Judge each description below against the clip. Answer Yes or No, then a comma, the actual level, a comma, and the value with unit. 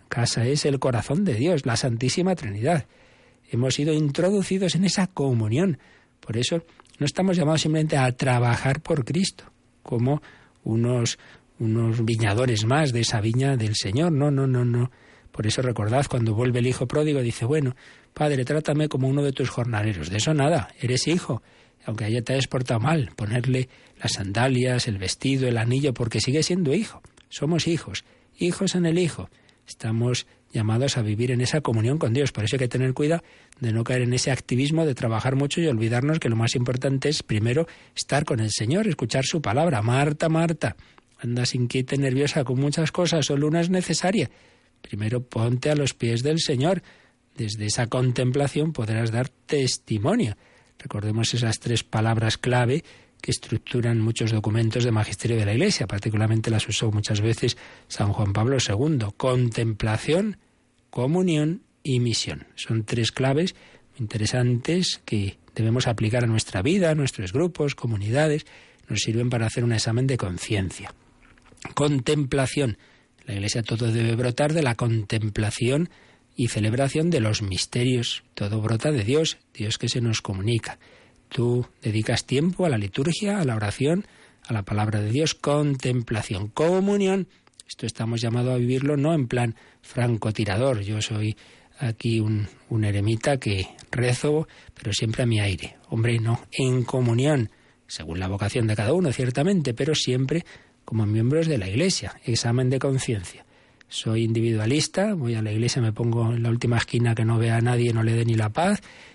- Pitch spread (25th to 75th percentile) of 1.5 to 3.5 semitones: No, average, 4.2 semitones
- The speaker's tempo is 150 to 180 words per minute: Yes, average, 165 wpm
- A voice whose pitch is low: Yes, low, 125 Hz